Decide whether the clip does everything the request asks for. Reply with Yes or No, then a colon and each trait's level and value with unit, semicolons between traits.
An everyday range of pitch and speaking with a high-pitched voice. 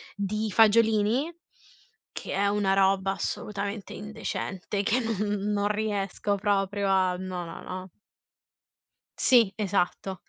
No: narrow, 1.7 semitones; high, 200 Hz